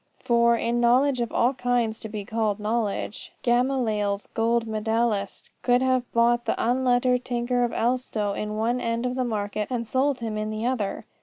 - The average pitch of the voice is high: Yes, high, 235 Hz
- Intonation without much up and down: Yes, narrow, 2.3 semitones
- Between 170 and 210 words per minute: Yes, average, 175 wpm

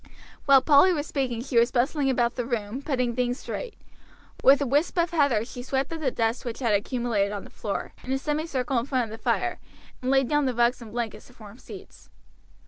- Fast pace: Yes, fast, 225 wpm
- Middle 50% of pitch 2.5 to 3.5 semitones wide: Yes, average, 2.9 semitones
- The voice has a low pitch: No, very high, 250 Hz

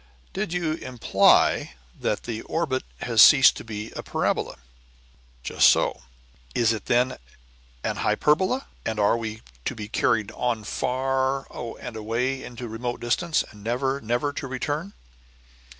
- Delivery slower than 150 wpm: Yes, average, 140 wpm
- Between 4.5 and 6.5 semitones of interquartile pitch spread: No, average, 3.4 semitones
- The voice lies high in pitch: No, low, 125 Hz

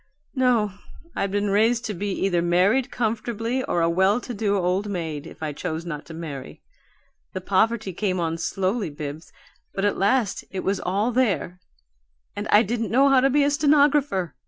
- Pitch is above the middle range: Yes, high, 200 Hz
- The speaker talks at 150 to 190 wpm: Yes, average, 180 wpm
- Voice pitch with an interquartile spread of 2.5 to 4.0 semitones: No, average, 5.1 semitones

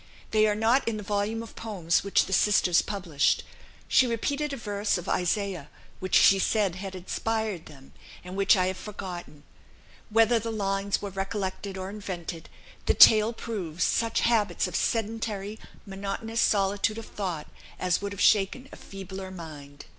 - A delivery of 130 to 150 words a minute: No, average, 160 wpm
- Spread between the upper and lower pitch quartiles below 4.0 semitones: Yes, average, 2.9 semitones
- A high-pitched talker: Yes, high, 200 Hz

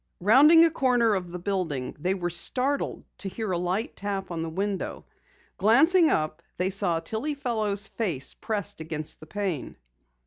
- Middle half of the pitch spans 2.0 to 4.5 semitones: No, average, 4.9 semitones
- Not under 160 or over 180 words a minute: Yes, average, 165 wpm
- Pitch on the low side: No, high, 200 Hz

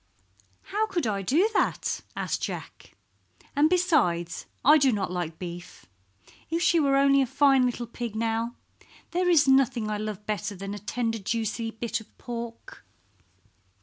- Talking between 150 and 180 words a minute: Yes, average, 155 wpm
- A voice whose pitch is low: No, high, 235 Hz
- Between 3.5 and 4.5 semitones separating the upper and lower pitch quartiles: No, average, 4.9 semitones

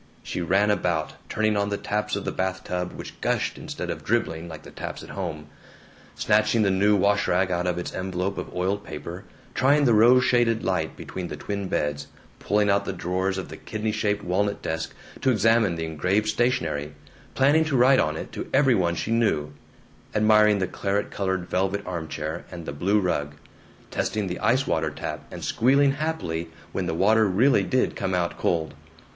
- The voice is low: Yes, very low, 95 Hz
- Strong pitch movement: No, average, 3.7 semitones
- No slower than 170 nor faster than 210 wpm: Yes, average, 190 wpm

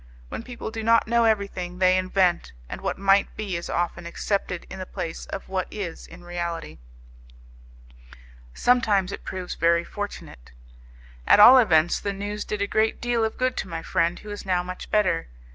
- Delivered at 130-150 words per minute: No, average, 180 wpm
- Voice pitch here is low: No, high, 190 Hz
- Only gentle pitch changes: No, average, 3.3 semitones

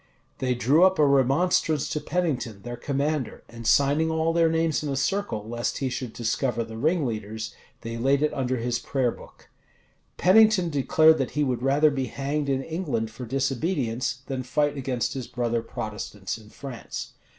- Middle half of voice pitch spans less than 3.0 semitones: No, average, 4.3 semitones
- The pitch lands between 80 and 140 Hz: Yes, low, 135 Hz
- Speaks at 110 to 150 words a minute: No, average, 175 wpm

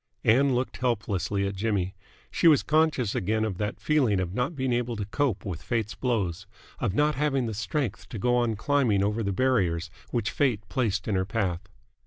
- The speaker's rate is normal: Yes, average, 195 wpm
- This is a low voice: Yes, low, 110 Hz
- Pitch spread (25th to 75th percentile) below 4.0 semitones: No, average, 4.6 semitones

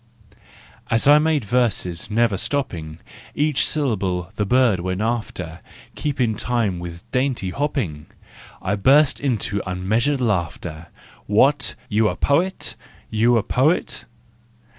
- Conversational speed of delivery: No, slow, 120 wpm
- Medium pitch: No, low, 110 Hz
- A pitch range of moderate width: No, wide, 6.6 semitones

